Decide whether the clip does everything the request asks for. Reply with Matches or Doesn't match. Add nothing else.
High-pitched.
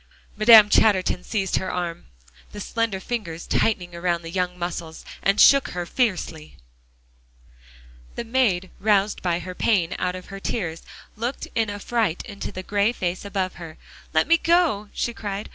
Matches